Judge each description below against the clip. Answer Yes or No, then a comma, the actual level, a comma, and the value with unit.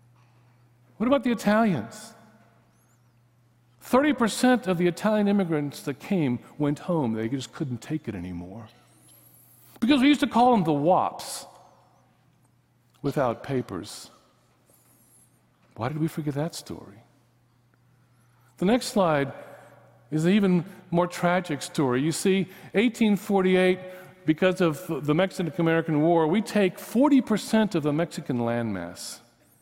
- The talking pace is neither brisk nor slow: No, slow, 120 wpm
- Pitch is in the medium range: Yes, medium, 160 Hz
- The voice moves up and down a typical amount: No, wide, 7.8 semitones